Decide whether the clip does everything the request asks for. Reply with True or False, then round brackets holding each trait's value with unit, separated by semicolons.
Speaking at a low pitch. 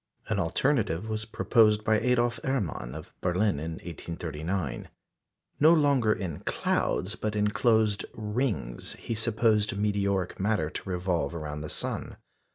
True (105 Hz)